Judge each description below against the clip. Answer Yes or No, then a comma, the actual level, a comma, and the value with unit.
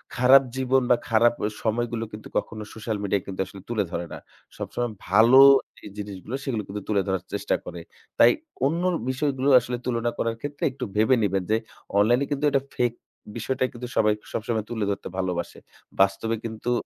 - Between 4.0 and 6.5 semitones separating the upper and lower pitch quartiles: No, average, 3.4 semitones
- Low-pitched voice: Yes, low, 115 Hz